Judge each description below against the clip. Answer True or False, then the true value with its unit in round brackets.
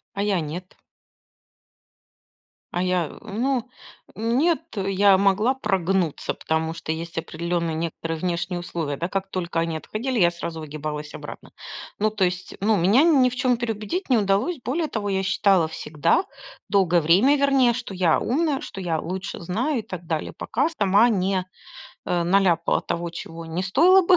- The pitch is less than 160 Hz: False (190 Hz)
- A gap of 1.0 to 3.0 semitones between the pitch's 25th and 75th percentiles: False (5.2 semitones)